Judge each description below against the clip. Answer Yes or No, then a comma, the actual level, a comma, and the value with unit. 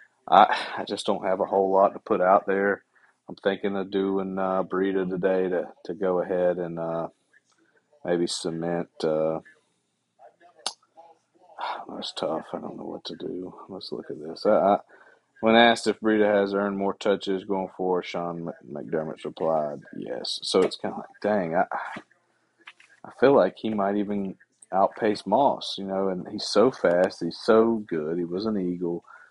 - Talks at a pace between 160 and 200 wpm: Yes, average, 170 wpm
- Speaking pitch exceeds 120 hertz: No, very low, 95 Hz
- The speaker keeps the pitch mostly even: Yes, narrow, 2.0 semitones